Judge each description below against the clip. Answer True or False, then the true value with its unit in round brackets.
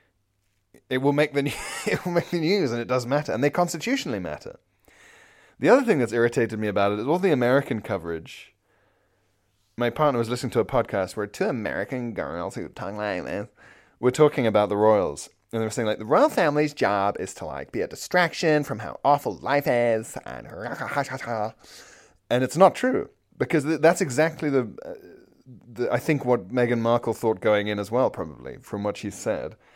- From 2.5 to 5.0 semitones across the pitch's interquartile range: False (5.6 semitones)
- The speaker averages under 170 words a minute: False (195 wpm)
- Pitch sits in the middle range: False (120 Hz)